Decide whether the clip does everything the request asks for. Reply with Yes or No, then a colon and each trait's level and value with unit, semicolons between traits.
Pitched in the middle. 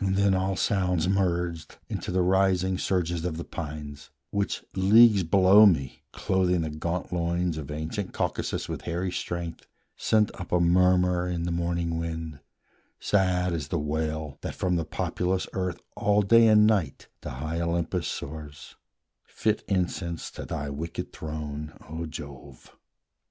No: very low, 85 Hz